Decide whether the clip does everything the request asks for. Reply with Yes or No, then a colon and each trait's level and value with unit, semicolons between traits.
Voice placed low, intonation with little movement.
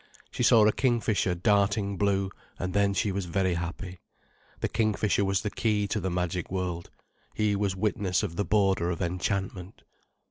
Yes: low, 100 Hz; narrow, 2.1 semitones